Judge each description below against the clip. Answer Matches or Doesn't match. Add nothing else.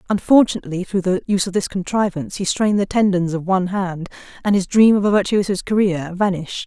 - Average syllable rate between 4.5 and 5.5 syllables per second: Doesn't match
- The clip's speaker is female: Matches